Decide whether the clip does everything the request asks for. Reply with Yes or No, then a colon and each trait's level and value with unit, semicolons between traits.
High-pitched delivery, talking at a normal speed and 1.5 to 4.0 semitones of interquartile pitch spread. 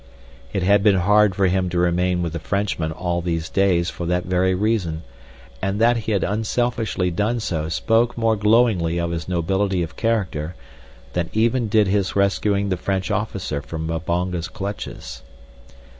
No: very low, 95 Hz; average, 165 wpm; average, 3.4 semitones